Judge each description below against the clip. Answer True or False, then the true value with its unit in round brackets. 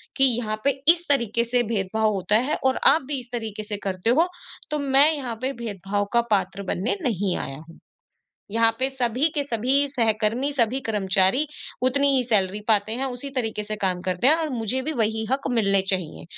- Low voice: False (230 Hz)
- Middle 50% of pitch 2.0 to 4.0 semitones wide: False (4.5 semitones)